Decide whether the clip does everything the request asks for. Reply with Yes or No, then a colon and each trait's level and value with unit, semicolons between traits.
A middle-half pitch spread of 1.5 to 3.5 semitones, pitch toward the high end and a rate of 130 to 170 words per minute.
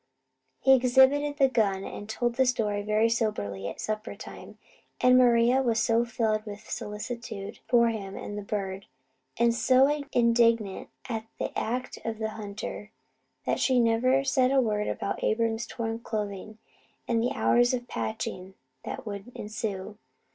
Yes: average, 2.7 semitones; high, 225 Hz; average, 155 wpm